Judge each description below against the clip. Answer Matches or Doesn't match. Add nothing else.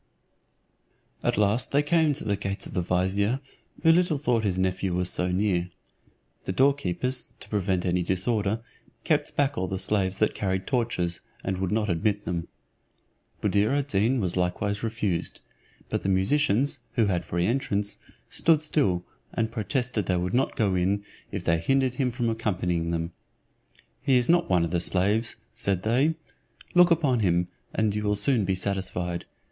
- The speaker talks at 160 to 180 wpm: Matches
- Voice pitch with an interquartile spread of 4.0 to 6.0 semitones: Matches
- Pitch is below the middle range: Matches